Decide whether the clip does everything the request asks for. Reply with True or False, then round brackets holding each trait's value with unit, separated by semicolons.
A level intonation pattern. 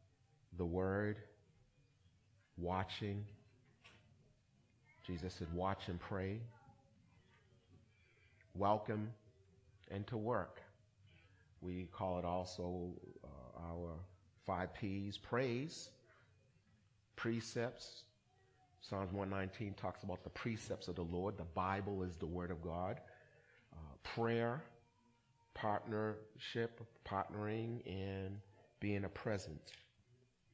False (3.9 semitones)